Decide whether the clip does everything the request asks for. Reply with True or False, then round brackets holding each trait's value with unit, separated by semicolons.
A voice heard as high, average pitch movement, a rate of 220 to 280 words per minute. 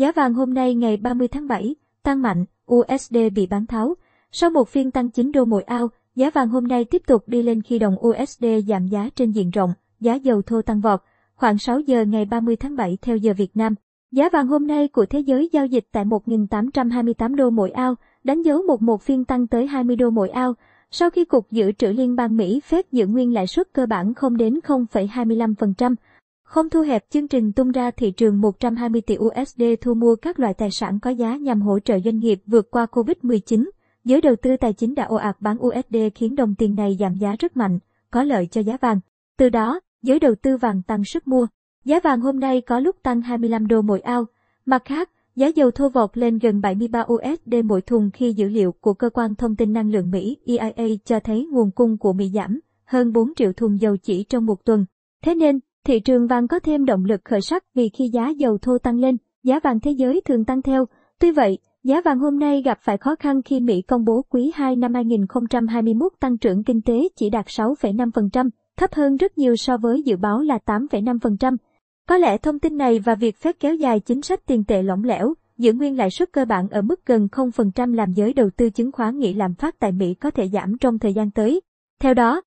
True (240 Hz; 3.2 semitones; 230 wpm)